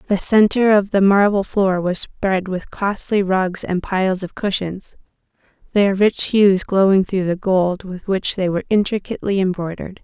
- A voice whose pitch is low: No, high, 190 Hz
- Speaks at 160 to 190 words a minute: Yes, average, 165 wpm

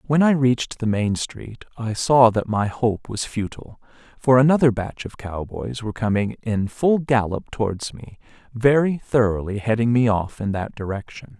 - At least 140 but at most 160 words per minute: No, average, 175 wpm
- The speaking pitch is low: Yes, low, 115 Hz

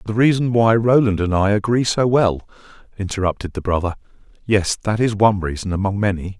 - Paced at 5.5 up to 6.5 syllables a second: Yes, 5.8 syllables/s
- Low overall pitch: Yes, low, 105 Hz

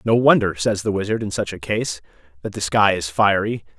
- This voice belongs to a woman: No, male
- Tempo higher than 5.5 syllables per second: No, 5.4 syllables/s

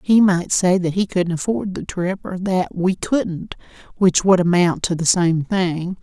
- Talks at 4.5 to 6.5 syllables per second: No, 4.0 syllables/s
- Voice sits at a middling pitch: Yes, medium, 180 Hz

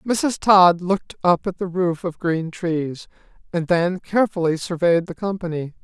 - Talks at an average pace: Yes, average, 165 wpm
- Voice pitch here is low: No, medium, 175 Hz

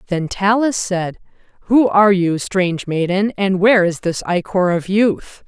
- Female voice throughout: Yes, female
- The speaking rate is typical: Yes, average, 165 wpm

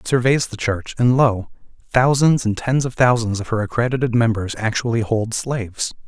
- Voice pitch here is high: No, low, 120 Hz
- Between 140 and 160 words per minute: No, average, 180 wpm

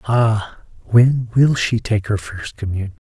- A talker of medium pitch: No, low, 110 Hz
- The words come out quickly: No, average, 155 wpm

